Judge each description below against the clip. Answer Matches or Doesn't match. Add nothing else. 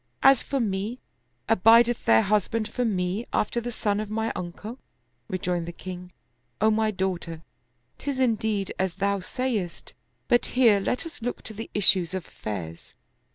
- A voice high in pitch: Matches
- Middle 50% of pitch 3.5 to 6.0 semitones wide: Matches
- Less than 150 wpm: Doesn't match